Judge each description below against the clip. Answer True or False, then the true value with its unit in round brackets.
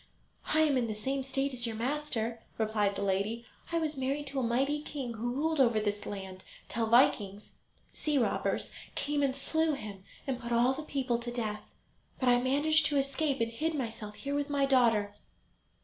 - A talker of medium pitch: False (255 Hz)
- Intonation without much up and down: False (4.1 semitones)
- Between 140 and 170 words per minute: False (195 wpm)